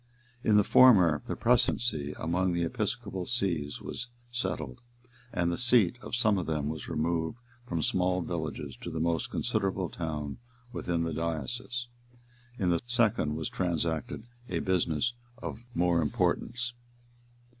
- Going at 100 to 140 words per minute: Yes, slow, 135 wpm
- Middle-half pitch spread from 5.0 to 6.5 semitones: Yes, wide, 5.6 semitones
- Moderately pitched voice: No, very low, 85 Hz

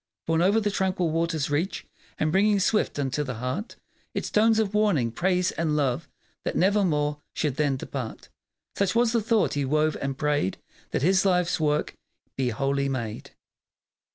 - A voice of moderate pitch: Yes, medium, 155 Hz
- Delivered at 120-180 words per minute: Yes, average, 165 wpm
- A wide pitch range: Yes, wide, 5.7 semitones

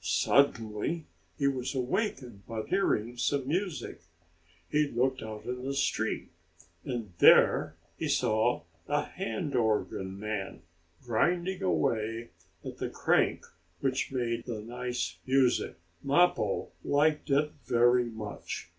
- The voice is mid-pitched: No, low, 125 Hz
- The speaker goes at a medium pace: No, slow, 120 wpm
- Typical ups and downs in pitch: Yes, average, 4.3 semitones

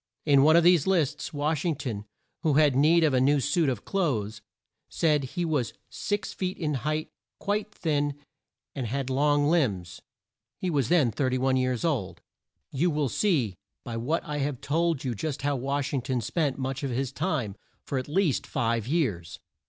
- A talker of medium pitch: Yes, medium, 145 Hz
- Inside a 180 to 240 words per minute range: Yes, average, 185 wpm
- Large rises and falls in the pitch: No, average, 3.7 semitones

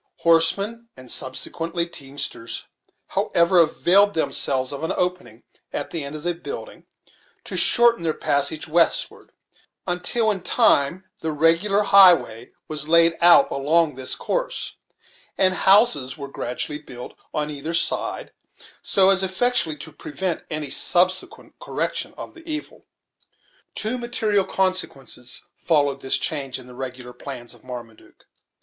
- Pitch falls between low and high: Yes, medium, 165 Hz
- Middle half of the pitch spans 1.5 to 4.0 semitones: No, average, 5.3 semitones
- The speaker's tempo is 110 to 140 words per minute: Yes, slow, 135 wpm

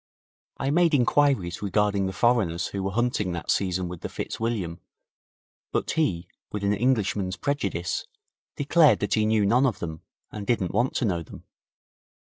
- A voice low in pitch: Yes, low, 105 Hz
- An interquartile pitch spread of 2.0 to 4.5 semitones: No, average, 5.0 semitones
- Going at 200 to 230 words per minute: No, average, 160 wpm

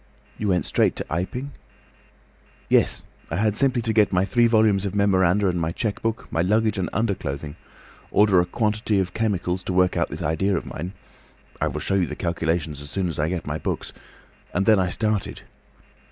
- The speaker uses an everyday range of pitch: Yes, average, 3.4 semitones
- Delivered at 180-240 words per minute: Yes, average, 190 wpm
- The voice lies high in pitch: No, very low, 95 Hz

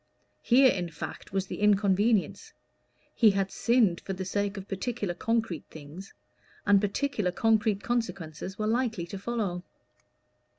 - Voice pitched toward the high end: Yes, high, 200 Hz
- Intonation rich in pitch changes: No, average, 3.2 semitones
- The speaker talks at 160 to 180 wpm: No, slow, 135 wpm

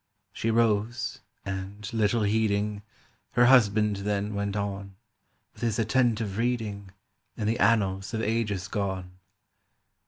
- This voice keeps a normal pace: No, slow, 120 wpm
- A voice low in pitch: Yes, low, 105 Hz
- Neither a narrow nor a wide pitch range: No, narrow, 2.2 semitones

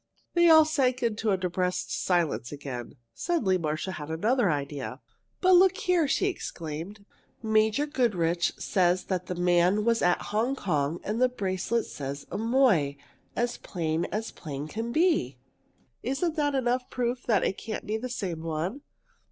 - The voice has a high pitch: Yes, high, 205 Hz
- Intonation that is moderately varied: No, wide, 7.0 semitones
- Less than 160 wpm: Yes, average, 150 wpm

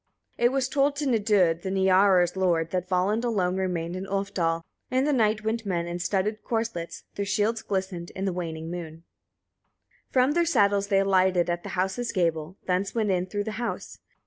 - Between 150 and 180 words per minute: No, average, 195 wpm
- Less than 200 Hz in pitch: Yes, high, 190 Hz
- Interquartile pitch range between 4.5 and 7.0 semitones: No, average, 3.6 semitones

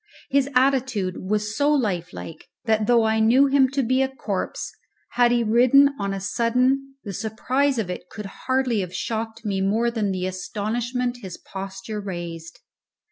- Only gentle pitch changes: No, average, 4.6 semitones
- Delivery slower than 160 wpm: No, average, 165 wpm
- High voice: Yes, high, 225 Hz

